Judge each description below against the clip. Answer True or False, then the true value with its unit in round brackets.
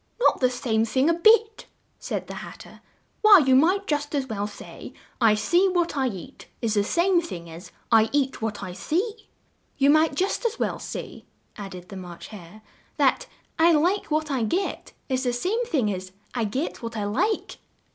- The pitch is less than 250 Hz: False (265 Hz)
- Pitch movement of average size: False (8.3 semitones)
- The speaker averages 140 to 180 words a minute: False (195 wpm)